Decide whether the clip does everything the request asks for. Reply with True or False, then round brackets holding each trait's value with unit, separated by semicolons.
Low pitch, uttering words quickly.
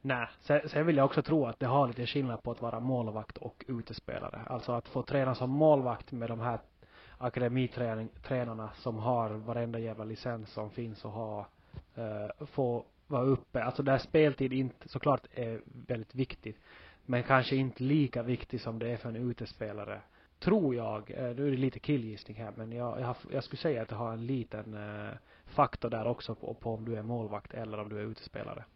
True (120 Hz; 200 wpm)